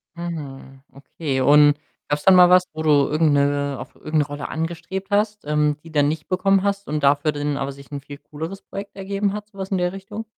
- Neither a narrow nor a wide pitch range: Yes, average, 4.9 semitones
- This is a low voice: No, medium, 155 Hz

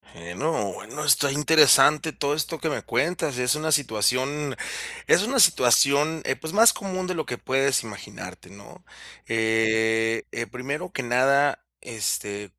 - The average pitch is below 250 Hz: Yes, medium, 140 Hz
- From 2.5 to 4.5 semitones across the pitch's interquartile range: No, wide, 5.4 semitones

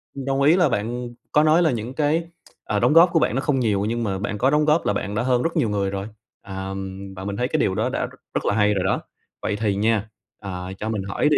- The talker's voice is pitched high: No, low, 115 Hz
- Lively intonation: Yes, wide, 6.2 semitones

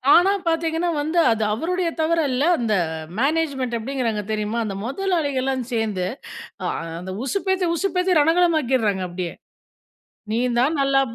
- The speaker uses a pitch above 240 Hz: Yes, very high, 275 Hz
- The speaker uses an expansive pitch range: Yes, wide, 6.7 semitones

